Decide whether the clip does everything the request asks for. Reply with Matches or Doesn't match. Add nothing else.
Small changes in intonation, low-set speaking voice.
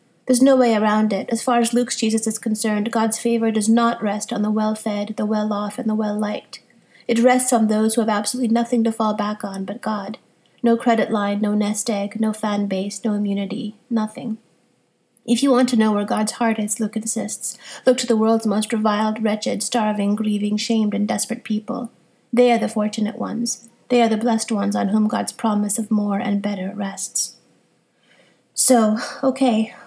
Doesn't match